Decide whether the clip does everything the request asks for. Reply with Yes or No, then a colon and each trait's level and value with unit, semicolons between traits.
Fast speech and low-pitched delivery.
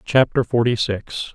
No: slow, 135 wpm; low, 115 Hz